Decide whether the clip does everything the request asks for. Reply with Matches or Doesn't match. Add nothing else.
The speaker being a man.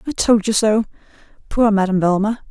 Doesn't match